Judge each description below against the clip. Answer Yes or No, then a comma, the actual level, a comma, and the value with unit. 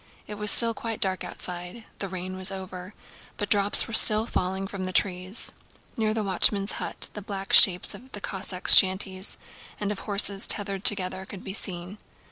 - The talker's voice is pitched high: Yes, high, 195 Hz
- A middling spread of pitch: No, narrow, 1.9 semitones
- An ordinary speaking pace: Yes, average, 180 wpm